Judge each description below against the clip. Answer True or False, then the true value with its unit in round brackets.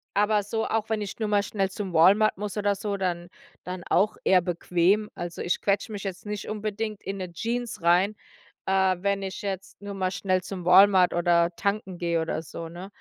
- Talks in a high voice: True (195 Hz)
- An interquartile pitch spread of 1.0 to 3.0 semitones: True (2.6 semitones)